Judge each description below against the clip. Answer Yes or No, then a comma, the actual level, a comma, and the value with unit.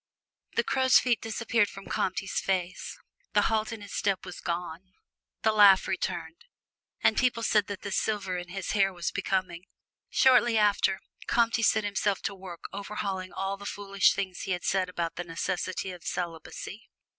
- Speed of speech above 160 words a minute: Yes, average, 170 wpm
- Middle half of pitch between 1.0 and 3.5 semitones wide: Yes, narrow, 2.5 semitones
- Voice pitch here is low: No, high, 195 Hz